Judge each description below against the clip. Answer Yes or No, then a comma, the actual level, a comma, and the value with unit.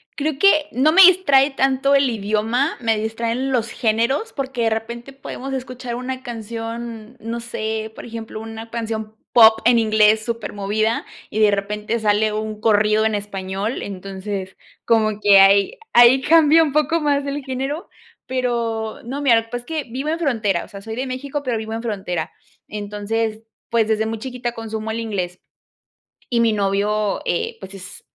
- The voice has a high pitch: Yes, high, 225 Hz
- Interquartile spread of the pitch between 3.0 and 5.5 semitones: Yes, average, 3.3 semitones